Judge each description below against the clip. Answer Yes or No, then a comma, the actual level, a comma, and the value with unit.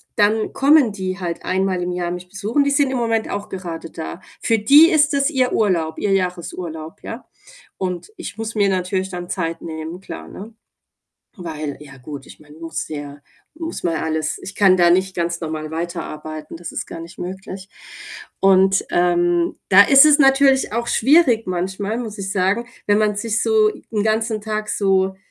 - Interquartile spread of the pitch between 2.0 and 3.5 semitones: No, average, 4.3 semitones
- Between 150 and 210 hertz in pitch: Yes, high, 190 Hz